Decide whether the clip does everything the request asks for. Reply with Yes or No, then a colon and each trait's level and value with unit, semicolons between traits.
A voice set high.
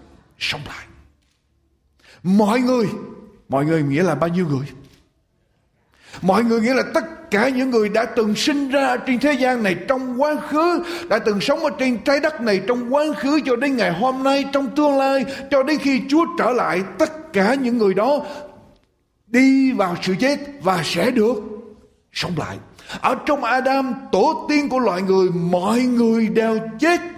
Yes: very high, 250 Hz